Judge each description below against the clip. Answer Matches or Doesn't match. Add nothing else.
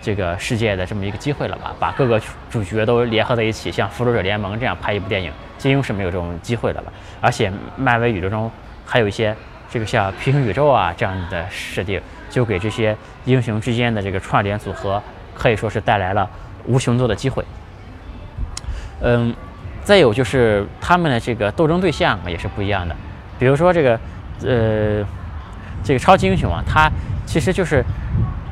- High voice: Doesn't match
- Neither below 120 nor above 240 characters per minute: Doesn't match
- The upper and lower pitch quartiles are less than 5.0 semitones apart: Matches